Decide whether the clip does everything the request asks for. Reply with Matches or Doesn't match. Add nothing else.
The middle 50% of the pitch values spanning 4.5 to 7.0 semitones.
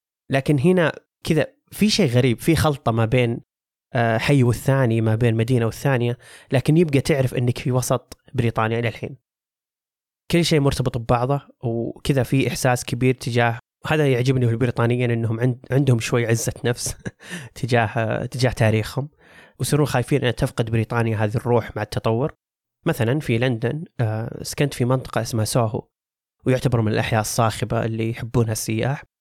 Doesn't match